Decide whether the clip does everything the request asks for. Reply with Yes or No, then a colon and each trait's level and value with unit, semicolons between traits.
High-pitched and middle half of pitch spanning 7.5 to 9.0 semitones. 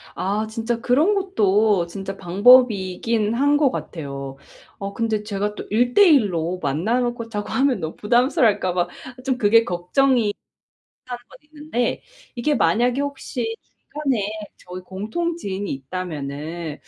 No: high, 215 Hz; average, 5.3 semitones